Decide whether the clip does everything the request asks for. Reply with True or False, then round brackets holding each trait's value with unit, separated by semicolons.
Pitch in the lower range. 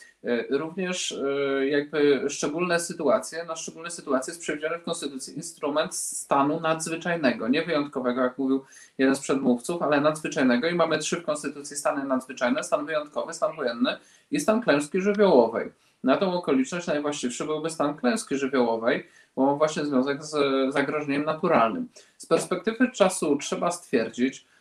False (150 Hz)